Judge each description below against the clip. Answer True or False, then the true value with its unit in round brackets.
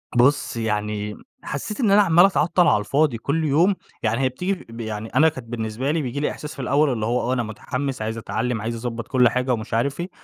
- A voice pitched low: True (125 Hz)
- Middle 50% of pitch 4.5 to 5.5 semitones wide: True (4.8 semitones)